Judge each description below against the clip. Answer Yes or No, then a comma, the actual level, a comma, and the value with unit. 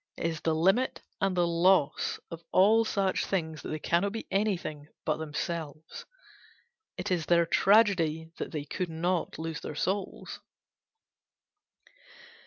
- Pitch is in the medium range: Yes, medium, 170 Hz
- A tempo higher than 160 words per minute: No, average, 140 wpm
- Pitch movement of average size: Yes, average, 3.3 semitones